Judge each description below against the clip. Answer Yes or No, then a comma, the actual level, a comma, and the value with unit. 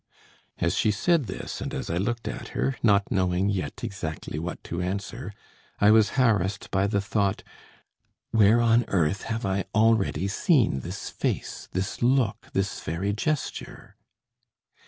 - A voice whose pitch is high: No, low, 100 Hz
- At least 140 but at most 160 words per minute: Yes, average, 150 wpm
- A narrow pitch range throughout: No, average, 3.3 semitones